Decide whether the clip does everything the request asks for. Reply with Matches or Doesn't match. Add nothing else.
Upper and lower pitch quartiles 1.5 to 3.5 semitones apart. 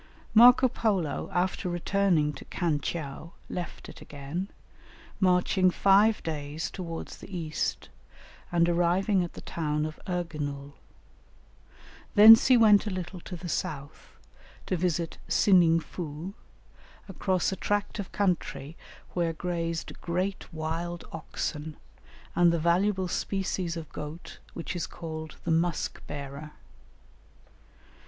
Matches